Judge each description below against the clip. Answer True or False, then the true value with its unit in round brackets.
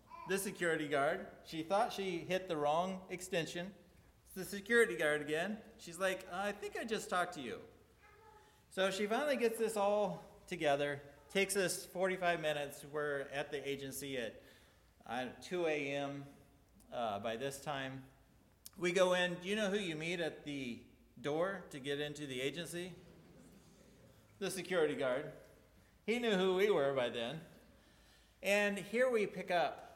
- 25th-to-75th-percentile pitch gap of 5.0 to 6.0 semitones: True (5.5 semitones)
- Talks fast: False (160 wpm)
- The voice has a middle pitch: True (175 Hz)